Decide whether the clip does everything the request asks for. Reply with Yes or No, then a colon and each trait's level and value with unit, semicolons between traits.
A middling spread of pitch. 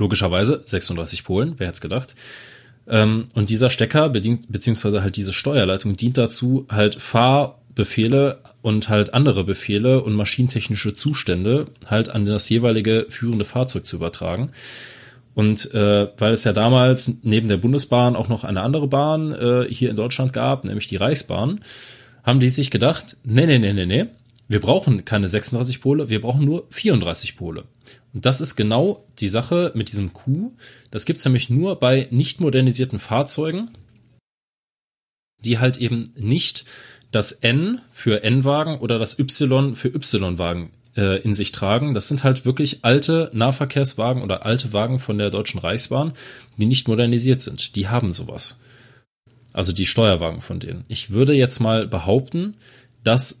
Yes: average, 3.8 semitones